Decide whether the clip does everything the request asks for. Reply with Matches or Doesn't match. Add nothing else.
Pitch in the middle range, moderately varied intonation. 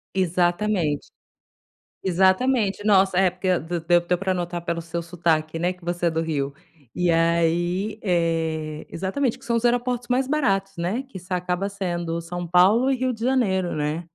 Matches